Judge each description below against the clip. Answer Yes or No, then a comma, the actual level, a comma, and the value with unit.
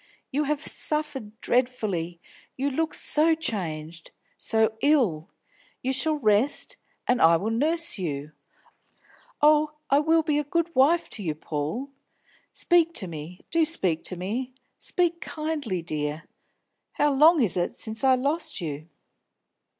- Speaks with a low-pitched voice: No, very high, 255 Hz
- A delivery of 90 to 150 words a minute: Yes, average, 140 wpm